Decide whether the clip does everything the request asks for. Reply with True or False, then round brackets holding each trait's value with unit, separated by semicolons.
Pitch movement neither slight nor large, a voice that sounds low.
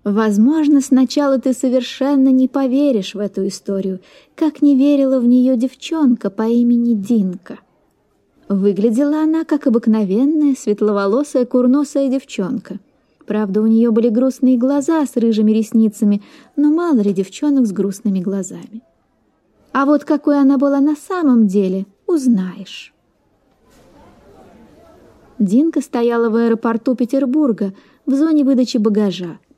False (4.7 semitones; 250 Hz)